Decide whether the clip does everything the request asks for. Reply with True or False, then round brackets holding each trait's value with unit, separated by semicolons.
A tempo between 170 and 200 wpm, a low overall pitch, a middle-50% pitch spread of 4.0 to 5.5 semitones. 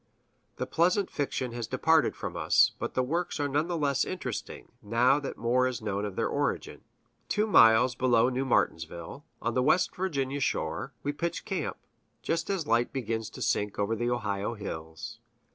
True (180 wpm; 125 Hz; 4.5 semitones)